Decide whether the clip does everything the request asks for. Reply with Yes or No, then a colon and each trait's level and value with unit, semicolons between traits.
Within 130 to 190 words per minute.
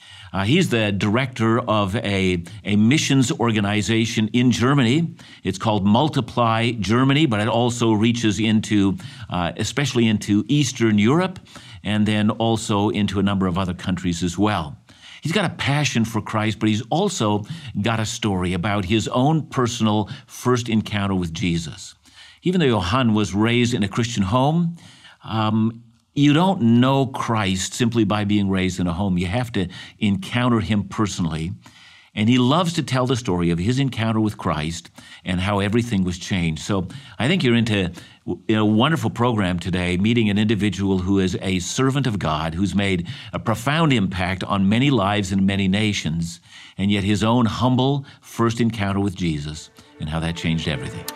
Yes: average, 170 wpm